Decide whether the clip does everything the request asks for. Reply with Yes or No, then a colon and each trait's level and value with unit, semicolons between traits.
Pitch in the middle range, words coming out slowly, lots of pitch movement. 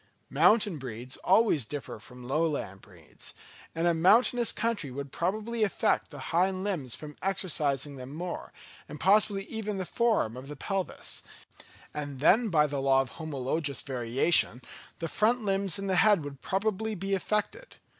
No: medium, 170 Hz; average, 155 wpm; wide, 6.8 semitones